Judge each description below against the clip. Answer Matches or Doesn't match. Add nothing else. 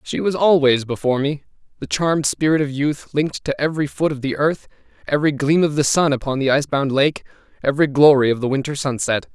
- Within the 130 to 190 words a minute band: Doesn't match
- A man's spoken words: Matches